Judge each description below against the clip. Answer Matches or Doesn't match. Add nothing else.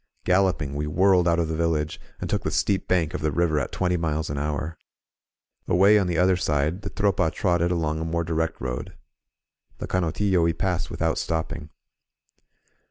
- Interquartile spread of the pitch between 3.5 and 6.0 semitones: Doesn't match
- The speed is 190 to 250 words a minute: Doesn't match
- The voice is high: Doesn't match